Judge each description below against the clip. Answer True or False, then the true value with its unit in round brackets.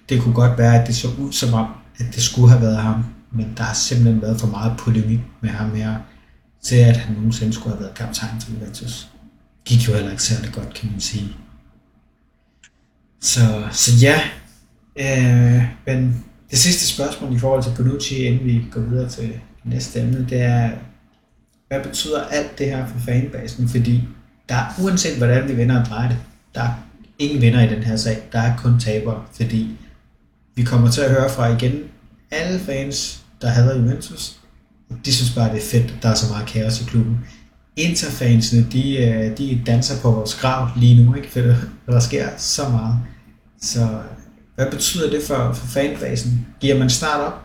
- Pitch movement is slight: True (2.3 semitones)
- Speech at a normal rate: True (190 wpm)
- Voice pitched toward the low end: True (120 Hz)